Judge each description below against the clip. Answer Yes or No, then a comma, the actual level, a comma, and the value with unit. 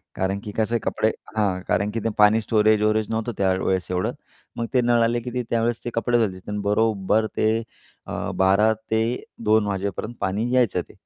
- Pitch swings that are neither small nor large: No, narrow, 2.3 semitones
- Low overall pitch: Yes, low, 110 Hz